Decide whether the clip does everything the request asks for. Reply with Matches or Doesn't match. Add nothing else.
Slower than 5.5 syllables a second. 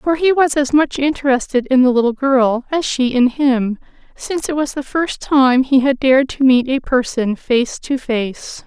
Matches